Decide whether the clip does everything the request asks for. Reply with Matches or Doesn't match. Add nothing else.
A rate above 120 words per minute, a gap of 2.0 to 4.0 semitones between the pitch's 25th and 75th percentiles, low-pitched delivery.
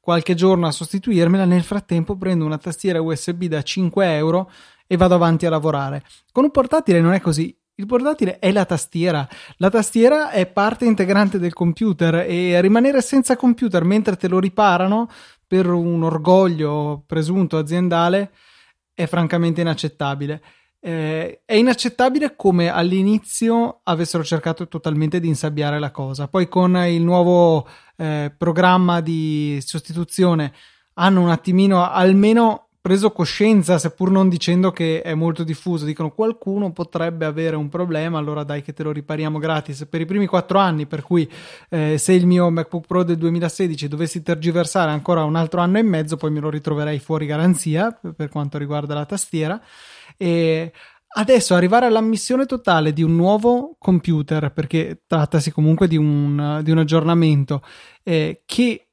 Doesn't match